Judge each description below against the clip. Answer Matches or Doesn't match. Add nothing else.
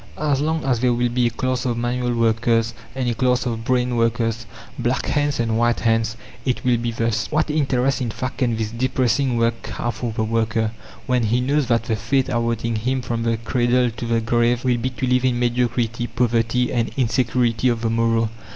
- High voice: Doesn't match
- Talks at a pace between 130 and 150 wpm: Doesn't match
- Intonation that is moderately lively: Doesn't match